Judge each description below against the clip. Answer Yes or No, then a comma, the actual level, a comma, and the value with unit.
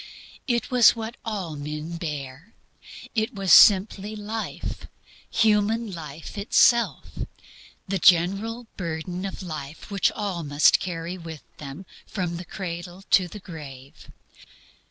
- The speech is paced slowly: Yes, slow, 120 wpm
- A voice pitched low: No, medium, 185 Hz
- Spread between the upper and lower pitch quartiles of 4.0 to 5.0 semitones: Yes, average, 4.5 semitones